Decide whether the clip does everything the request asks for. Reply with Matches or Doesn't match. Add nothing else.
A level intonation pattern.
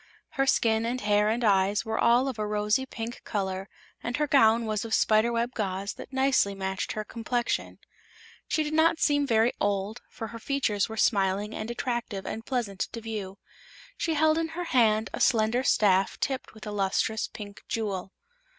Doesn't match